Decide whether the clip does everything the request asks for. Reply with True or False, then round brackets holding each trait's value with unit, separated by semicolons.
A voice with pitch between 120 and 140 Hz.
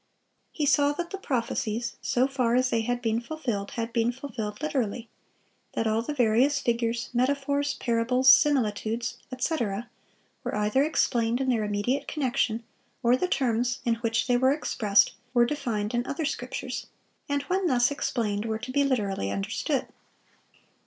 False (245 Hz)